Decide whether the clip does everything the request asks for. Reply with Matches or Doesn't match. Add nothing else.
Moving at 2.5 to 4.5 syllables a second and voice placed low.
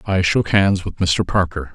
Matches